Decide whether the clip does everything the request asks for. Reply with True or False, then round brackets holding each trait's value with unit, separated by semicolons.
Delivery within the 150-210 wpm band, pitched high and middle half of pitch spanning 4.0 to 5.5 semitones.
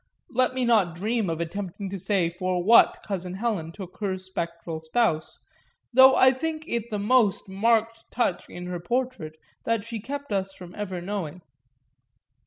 True (165 wpm; 200 Hz; 4.6 semitones)